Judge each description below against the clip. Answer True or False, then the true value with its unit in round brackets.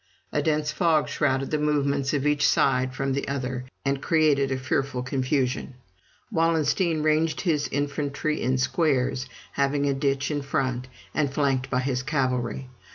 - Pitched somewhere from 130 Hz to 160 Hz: True (140 Hz)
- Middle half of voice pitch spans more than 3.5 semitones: False (2.4 semitones)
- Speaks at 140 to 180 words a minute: True (155 wpm)